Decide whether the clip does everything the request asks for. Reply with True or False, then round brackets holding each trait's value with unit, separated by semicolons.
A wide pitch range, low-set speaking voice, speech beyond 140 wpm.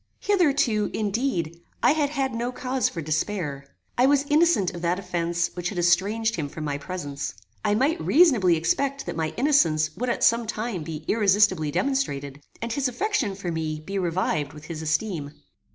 False (7.8 semitones; 190 Hz; 175 wpm)